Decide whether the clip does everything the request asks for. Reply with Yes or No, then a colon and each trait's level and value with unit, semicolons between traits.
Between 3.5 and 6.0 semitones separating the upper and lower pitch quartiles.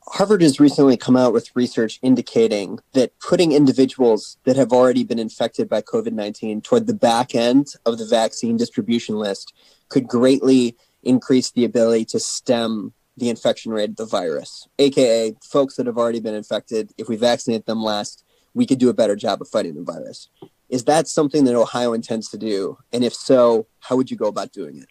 No: average, 3.1 semitones